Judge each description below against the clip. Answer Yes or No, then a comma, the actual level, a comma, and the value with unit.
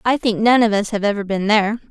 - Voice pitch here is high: Yes, high, 215 Hz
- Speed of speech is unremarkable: No, fast, 285 wpm